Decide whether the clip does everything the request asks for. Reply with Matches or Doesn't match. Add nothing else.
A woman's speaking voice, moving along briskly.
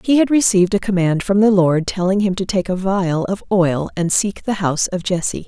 Matches